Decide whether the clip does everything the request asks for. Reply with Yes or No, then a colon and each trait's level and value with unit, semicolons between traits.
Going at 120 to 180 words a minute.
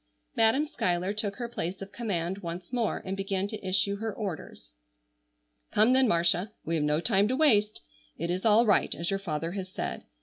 No: average, 195 wpm